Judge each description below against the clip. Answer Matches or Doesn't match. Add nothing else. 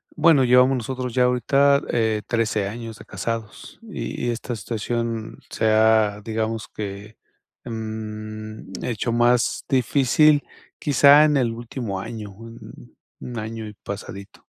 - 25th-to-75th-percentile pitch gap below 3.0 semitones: Matches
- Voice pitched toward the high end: Doesn't match